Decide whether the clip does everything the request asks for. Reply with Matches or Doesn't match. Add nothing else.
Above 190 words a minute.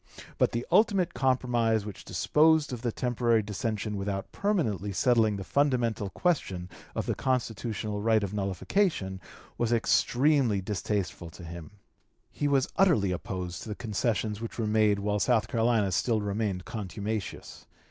Doesn't match